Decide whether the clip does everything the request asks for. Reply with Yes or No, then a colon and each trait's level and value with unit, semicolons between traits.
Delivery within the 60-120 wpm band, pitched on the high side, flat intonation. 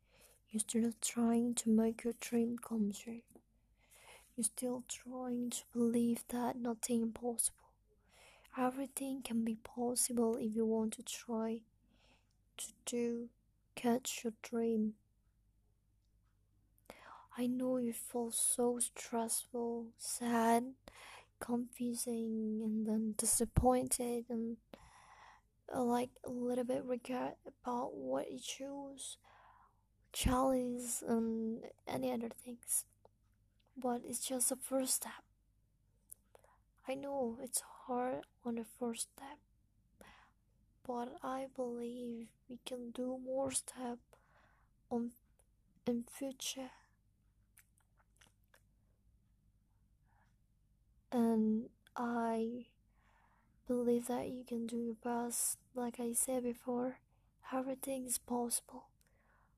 Yes: average, 100 wpm; high, 235 Hz; narrow, 1.9 semitones